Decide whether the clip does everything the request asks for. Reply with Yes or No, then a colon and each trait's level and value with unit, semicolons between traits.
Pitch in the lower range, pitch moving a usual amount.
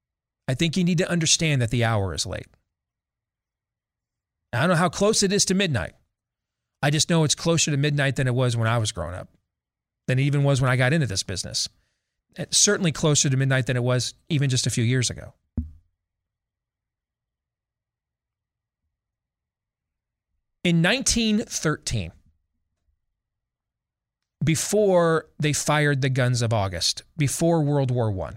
No: low, 130 Hz; wide, 6.9 semitones